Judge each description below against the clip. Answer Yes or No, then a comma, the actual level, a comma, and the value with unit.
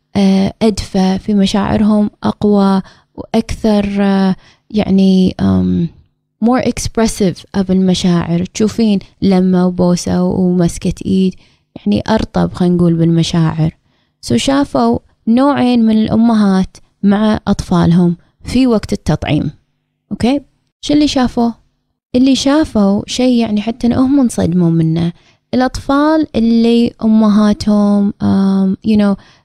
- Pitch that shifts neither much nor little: Yes, average, 4.1 semitones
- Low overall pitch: No, high, 205 Hz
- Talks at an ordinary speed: Yes, average, 100 wpm